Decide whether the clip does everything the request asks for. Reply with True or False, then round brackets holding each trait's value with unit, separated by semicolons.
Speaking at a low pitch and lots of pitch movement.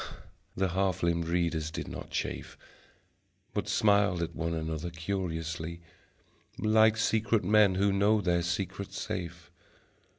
False (90 Hz; 3.2 semitones)